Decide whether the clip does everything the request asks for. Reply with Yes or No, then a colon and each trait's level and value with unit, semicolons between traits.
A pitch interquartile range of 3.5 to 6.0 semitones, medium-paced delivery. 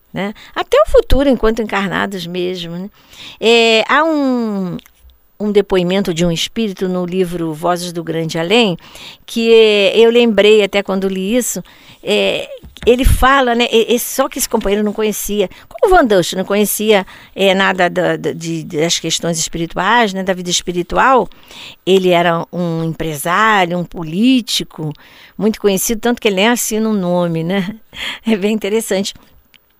Yes: average, 4.3 semitones; average, 165 wpm